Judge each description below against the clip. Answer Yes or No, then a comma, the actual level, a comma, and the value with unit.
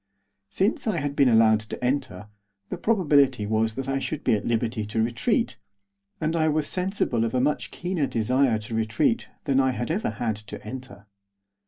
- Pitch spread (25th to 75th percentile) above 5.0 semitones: Yes, wide, 5.5 semitones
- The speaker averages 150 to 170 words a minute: No, average, 185 wpm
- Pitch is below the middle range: Yes, low, 125 Hz